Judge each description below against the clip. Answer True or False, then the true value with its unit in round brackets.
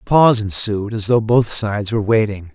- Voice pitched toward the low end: True (110 Hz)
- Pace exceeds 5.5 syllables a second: True (5.8 syllables/s)